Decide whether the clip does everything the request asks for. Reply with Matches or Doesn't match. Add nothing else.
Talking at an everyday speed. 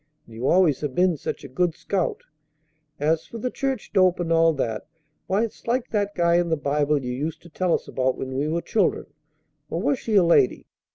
Doesn't match